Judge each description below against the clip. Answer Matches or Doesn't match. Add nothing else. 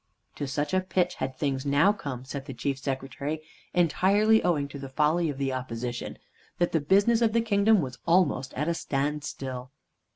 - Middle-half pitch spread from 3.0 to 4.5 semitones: Doesn't match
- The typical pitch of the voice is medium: Matches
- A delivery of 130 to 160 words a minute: Doesn't match